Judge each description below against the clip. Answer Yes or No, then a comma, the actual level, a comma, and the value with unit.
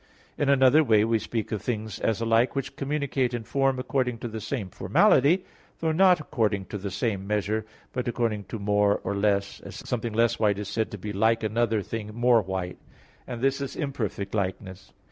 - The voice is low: Yes, low, 110 Hz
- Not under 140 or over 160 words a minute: No, average, 195 wpm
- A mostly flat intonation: No, average, 3.6 semitones